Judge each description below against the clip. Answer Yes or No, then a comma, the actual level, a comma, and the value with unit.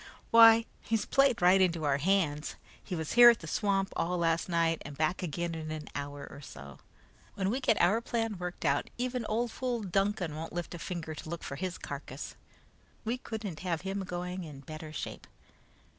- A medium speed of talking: Yes, average, 195 wpm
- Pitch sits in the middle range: Yes, medium, 180 Hz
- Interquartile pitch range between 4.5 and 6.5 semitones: Yes, average, 5.3 semitones